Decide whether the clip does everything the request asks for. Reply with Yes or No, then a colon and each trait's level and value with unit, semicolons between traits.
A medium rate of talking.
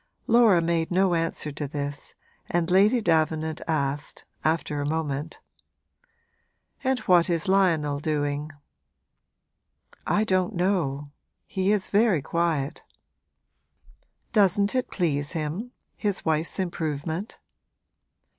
No: slow, 105 wpm